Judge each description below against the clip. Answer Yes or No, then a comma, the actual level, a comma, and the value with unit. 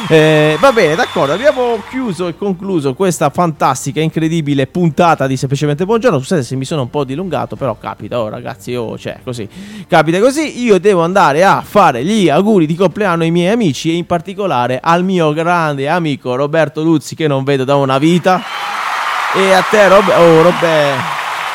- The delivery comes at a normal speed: No, fast, 180 wpm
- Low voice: No, medium, 165 Hz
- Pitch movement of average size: Yes, average, 4.6 semitones